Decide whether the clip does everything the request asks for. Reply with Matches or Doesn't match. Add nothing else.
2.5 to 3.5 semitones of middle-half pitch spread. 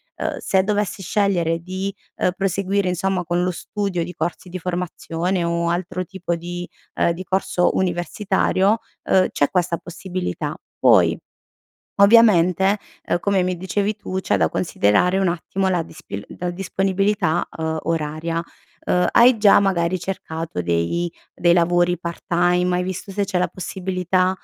Doesn't match